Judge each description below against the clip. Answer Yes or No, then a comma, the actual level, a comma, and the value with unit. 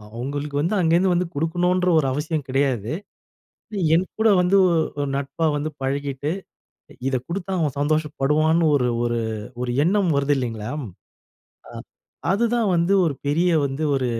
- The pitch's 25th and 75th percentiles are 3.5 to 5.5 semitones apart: Yes, average, 4.1 semitones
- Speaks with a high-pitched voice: No, medium, 150 Hz